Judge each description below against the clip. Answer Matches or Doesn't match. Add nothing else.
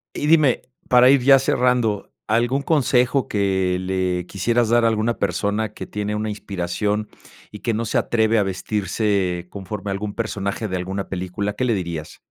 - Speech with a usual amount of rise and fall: Matches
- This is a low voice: Matches